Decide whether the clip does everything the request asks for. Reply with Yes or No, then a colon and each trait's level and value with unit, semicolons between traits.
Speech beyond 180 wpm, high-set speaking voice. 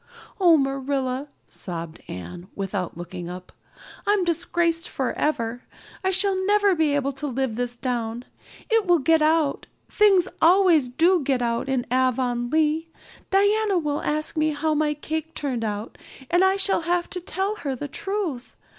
No: average, 155 wpm; very high, 300 Hz